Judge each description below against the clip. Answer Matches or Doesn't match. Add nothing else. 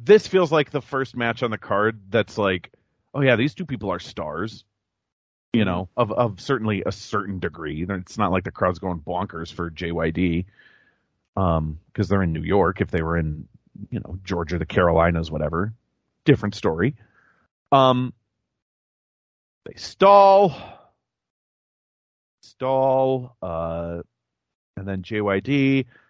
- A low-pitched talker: Matches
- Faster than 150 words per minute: Doesn't match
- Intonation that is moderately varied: Doesn't match